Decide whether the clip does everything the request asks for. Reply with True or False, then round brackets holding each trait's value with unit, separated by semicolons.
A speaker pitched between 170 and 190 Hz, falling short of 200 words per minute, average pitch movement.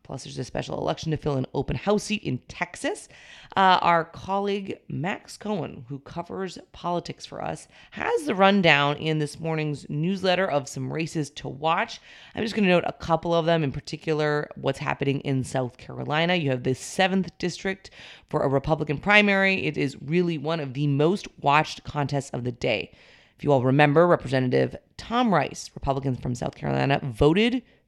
False (155 Hz; 180 wpm; 4.5 semitones)